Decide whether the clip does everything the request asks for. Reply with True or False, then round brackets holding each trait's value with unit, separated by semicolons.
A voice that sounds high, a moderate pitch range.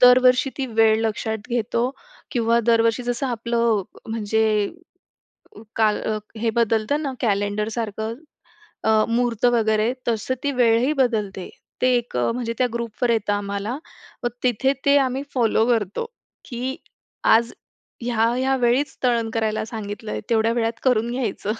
False (230 Hz; 2.1 semitones)